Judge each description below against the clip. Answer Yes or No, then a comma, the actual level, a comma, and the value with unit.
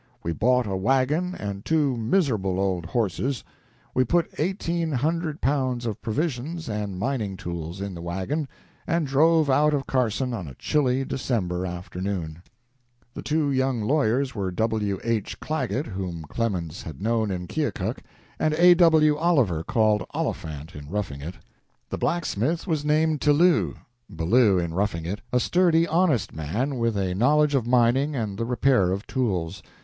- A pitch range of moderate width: No, wide, 7.6 semitones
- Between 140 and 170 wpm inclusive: Yes, average, 155 wpm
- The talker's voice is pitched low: Yes, low, 120 Hz